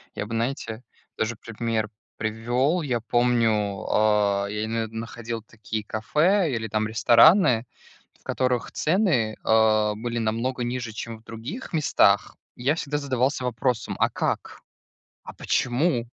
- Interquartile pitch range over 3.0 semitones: No, narrow, 2.6 semitones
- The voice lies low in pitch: Yes, low, 115 Hz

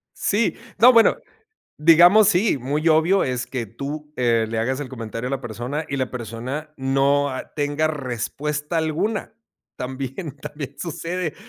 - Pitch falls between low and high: Yes, medium, 145 Hz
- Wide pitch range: No, average, 3.8 semitones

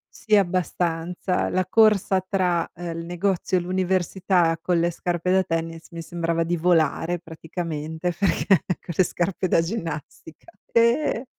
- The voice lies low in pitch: No, medium, 175 Hz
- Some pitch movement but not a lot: No, narrow, 2.1 semitones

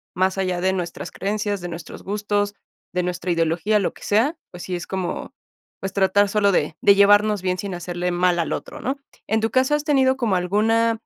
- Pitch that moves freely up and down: No, average, 3.0 semitones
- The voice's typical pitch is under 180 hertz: No, high, 195 Hz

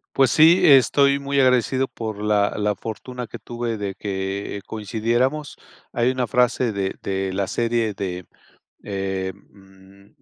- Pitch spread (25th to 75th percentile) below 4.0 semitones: No, average, 4.5 semitones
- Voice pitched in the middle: No, low, 110 Hz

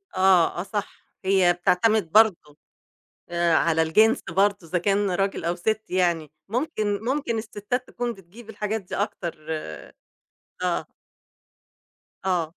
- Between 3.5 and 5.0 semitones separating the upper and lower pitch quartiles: Yes, average, 3.9 semitones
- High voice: Yes, high, 195 Hz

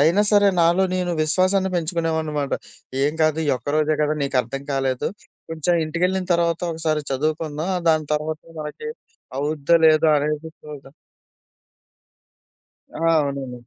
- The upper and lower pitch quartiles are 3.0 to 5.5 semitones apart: No, narrow, 2.5 semitones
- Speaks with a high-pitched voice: No, medium, 155 Hz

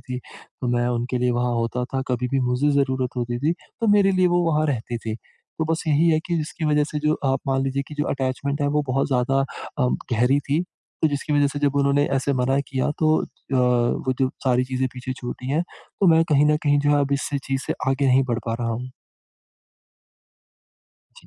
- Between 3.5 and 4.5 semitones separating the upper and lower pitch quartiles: No, average, 2.8 semitones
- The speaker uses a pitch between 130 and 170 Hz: Yes, low, 135 Hz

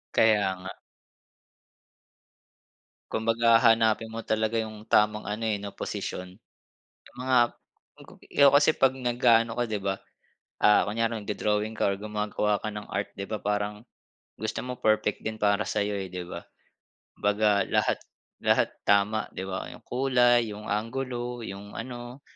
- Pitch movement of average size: No, narrow, 2.1 semitones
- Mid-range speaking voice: No, low, 110 Hz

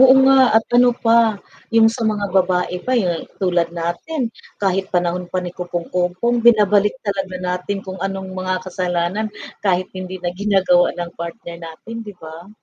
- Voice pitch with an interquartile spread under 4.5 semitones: Yes, average, 3.3 semitones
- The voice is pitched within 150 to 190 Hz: Yes, medium, 185 Hz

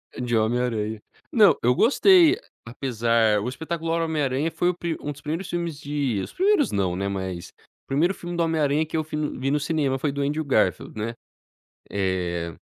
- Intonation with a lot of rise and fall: Yes, wide, 6.4 semitones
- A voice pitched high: No, medium, 140 Hz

